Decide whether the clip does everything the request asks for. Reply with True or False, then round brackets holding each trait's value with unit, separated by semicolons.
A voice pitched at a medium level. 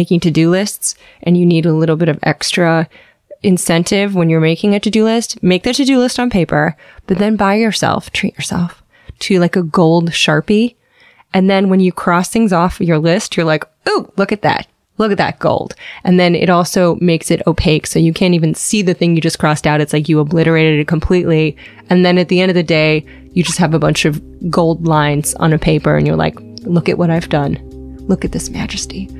True (170 Hz)